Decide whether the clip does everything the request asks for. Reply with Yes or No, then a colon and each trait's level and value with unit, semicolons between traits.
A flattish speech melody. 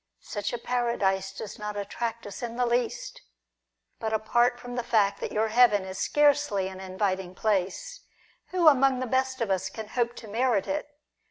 No: average, 3.7 semitones